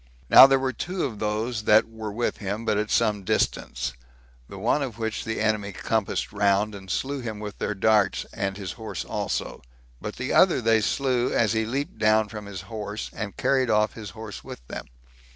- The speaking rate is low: No, average, 200 wpm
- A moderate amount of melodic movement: No, narrow, 2.0 semitones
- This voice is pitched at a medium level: No, low, 110 Hz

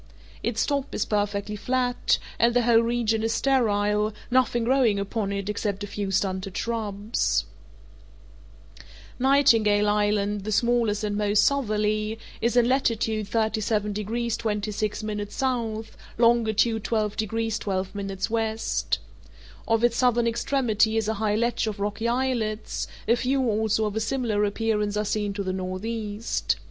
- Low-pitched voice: No, high, 220 Hz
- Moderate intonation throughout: No, narrow, 2.2 semitones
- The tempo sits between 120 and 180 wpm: Yes, average, 140 wpm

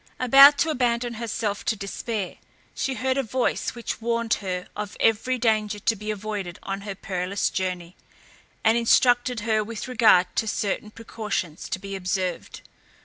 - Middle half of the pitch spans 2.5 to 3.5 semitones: Yes, average, 3.1 semitones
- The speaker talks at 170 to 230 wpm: No, average, 155 wpm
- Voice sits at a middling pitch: No, high, 215 Hz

